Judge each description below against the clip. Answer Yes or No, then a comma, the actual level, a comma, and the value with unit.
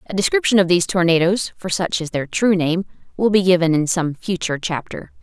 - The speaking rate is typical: Yes, average, 185 wpm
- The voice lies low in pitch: No, medium, 180 Hz